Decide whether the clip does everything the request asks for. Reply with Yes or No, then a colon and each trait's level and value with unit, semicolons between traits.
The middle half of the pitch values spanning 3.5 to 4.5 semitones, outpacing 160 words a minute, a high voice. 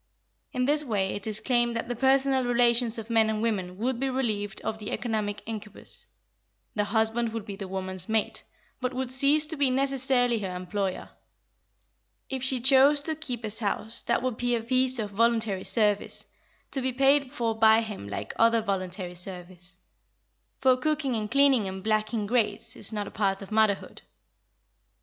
Yes: average, 3.8 semitones; average, 175 wpm; high, 225 Hz